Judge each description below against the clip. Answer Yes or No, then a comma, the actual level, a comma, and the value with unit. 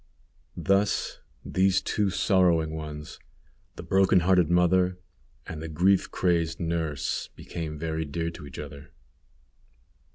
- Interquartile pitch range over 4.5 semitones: No, average, 2.8 semitones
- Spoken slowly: Yes, slow, 120 wpm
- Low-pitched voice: Yes, very low, 85 Hz